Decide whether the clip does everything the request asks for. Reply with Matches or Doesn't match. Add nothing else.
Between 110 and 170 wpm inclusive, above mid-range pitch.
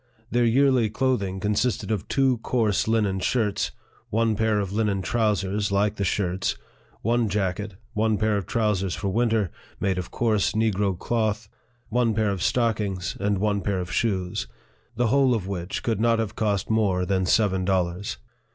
Doesn't match